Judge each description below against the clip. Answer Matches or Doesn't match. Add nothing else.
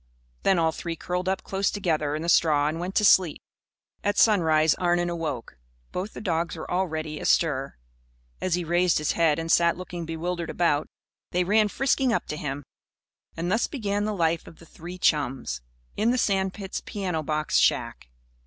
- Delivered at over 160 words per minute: Matches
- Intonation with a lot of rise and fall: Doesn't match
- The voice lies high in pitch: Doesn't match